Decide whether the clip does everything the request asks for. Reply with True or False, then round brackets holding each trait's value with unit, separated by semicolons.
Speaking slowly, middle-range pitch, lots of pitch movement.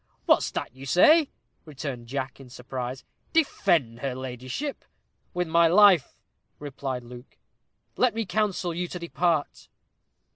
True (125 wpm; 145 Hz; 5.8 semitones)